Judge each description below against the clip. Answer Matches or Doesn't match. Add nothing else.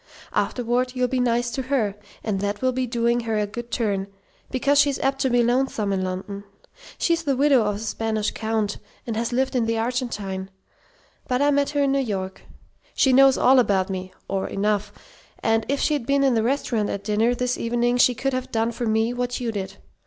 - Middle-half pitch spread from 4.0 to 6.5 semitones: Doesn't match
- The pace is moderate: Doesn't match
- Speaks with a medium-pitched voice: Doesn't match